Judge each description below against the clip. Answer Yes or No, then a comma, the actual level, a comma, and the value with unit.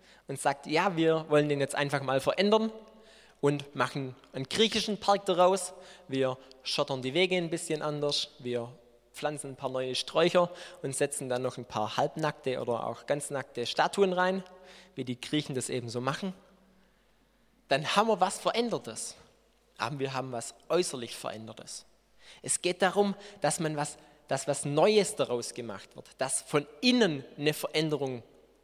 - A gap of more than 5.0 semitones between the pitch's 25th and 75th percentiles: Yes, wide, 5.6 semitones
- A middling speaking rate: Yes, average, 160 wpm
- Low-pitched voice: No, medium, 150 Hz